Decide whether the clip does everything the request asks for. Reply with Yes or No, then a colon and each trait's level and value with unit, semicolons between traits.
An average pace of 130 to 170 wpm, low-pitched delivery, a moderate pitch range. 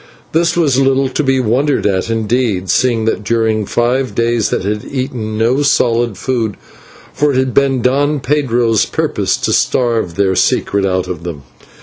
Yes: average, 165 wpm; low, 120 Hz; average, 3.7 semitones